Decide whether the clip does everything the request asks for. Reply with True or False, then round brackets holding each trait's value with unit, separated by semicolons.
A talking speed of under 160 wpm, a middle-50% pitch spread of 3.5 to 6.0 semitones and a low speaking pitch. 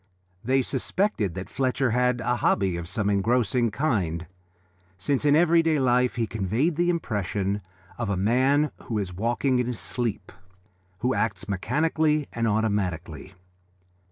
True (140 wpm; 5.0 semitones; 120 Hz)